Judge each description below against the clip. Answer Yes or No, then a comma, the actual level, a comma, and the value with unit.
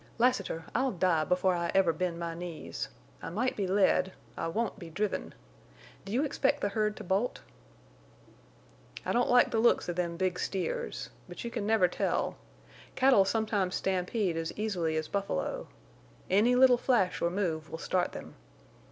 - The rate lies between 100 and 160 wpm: No, average, 170 wpm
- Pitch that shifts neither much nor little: Yes, average, 4.7 semitones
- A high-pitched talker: Yes, high, 195 Hz